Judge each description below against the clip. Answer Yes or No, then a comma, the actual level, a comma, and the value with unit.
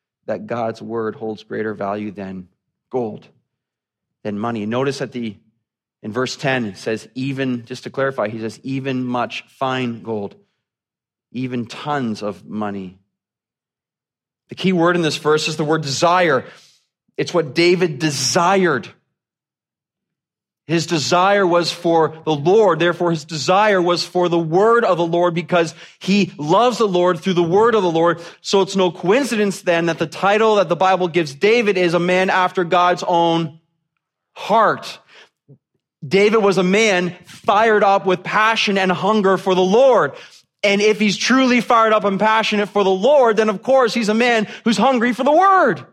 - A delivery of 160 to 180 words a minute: Yes, average, 165 wpm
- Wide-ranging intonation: Yes, wide, 7.1 semitones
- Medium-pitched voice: Yes, medium, 175 Hz